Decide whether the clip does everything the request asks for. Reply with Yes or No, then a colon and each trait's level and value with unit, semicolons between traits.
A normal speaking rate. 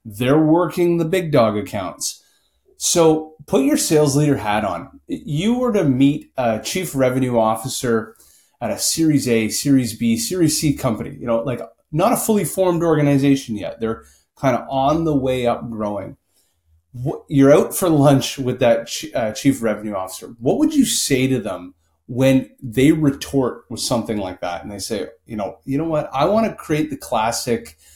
Yes: average, 180 wpm